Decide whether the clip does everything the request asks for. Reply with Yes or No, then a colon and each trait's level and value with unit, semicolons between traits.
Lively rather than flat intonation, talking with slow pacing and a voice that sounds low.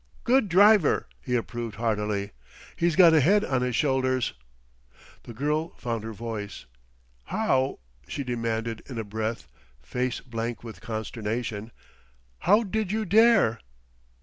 Yes: wide, 6.9 semitones; slow, 130 wpm; low, 125 Hz